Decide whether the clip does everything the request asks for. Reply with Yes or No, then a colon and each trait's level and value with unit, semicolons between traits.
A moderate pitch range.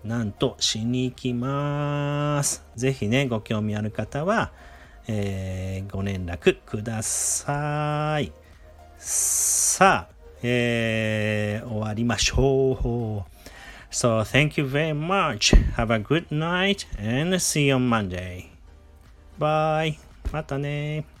No: wide, 7.1 semitones